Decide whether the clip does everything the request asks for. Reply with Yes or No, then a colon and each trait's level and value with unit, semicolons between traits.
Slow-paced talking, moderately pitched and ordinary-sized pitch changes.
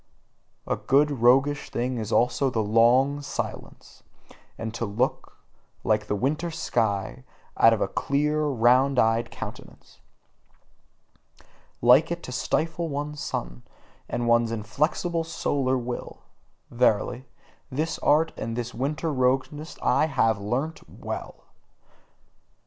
No: slow, 120 wpm; low, 130 Hz; average, 4.2 semitones